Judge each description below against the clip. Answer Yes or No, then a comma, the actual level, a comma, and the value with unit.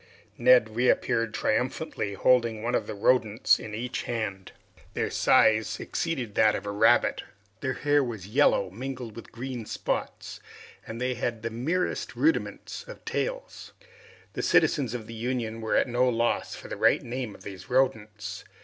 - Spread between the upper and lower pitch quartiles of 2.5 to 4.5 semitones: Yes, average, 2.8 semitones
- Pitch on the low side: Yes, low, 120 Hz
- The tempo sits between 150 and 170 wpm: Yes, average, 160 wpm